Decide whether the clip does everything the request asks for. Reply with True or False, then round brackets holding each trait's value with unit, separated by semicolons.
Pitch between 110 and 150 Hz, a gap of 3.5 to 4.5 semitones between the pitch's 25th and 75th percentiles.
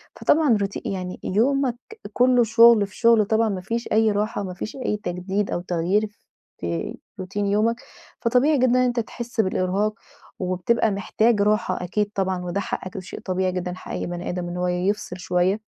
False (205 Hz; 3.8 semitones)